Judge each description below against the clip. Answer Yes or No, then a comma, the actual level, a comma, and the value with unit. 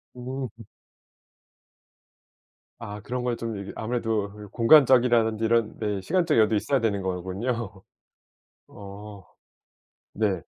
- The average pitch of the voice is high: No, low, 110 Hz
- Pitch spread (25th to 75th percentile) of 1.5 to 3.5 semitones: Yes, average, 3.2 semitones